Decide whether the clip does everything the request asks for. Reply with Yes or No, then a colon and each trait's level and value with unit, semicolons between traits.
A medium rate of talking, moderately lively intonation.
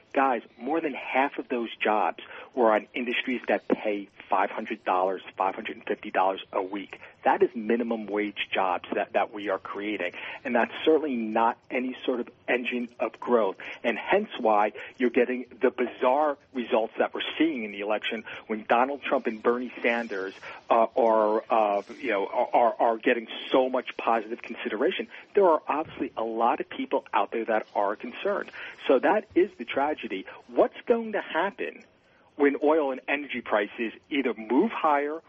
Yes: average, 165 wpm; average, 4.2 semitones